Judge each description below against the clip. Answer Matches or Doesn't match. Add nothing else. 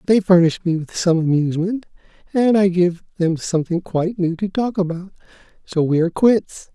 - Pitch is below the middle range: Doesn't match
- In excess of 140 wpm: Matches